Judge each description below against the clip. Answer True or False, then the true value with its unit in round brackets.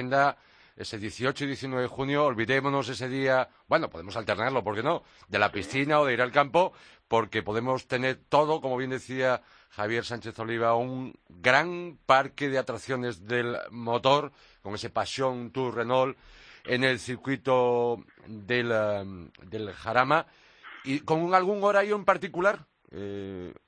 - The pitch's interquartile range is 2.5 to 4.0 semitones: True (3.2 semitones)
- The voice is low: True (130 Hz)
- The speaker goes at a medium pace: True (150 wpm)